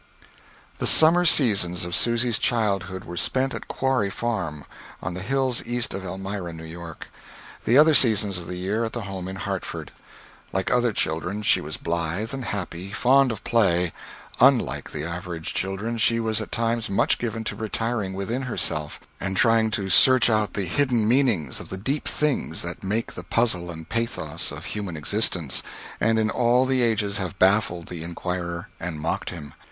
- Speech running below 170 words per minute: No, average, 180 wpm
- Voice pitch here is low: Yes, low, 100 Hz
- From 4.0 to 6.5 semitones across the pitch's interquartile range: Yes, average, 4.9 semitones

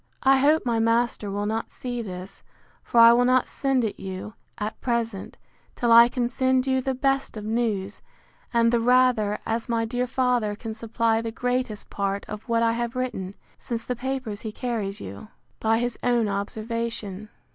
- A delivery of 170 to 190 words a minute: Yes, average, 180 wpm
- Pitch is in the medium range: No, high, 230 Hz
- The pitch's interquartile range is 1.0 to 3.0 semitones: Yes, narrow, 2.6 semitones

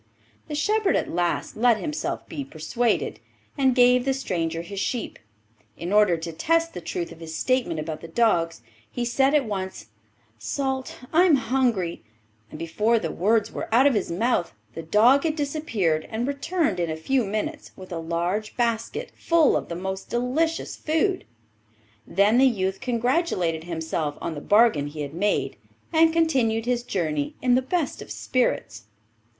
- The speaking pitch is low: No, high, 225 Hz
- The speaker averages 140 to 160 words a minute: No, average, 170 wpm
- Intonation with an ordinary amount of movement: No, wide, 7.9 semitones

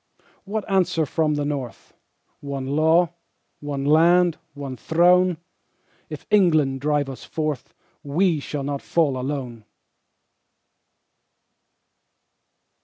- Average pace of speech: No, slow, 100 wpm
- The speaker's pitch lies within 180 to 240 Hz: No, medium, 150 Hz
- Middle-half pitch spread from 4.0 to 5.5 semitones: No, average, 3.5 semitones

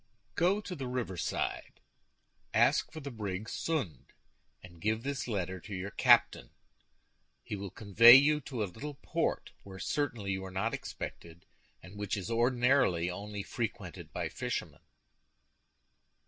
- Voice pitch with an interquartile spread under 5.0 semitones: No, average, 5.3 semitones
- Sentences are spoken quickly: No, average, 140 wpm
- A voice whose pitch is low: Yes, low, 105 Hz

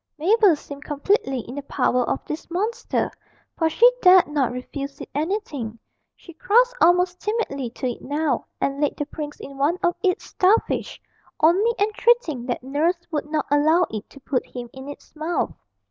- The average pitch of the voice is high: Yes, very high, 305 Hz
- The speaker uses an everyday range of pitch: Yes, average, 4.8 semitones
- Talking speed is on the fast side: No, average, 175 wpm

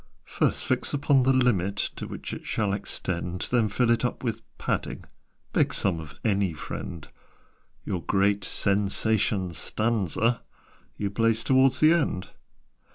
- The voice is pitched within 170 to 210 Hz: No, low, 105 Hz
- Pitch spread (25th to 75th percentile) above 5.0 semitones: No, average, 4.1 semitones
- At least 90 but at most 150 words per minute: Yes, average, 140 wpm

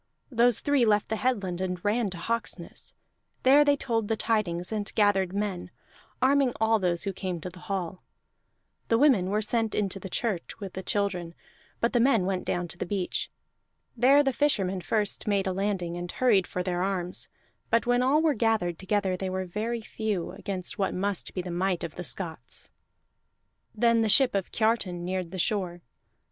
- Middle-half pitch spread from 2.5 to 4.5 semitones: Yes, average, 3.9 semitones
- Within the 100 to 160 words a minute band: No, average, 185 wpm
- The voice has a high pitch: Yes, high, 200 Hz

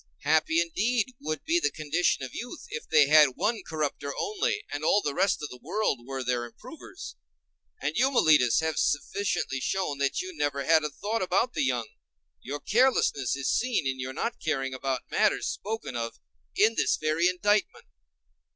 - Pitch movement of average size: No, wide, 7.5 semitones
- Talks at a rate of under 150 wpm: No, average, 180 wpm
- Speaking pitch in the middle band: Yes, medium, 155 Hz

